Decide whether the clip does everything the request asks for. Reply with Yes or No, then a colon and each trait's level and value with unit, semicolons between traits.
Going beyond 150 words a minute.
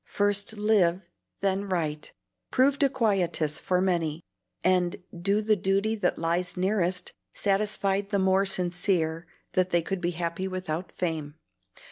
No: slow, 135 wpm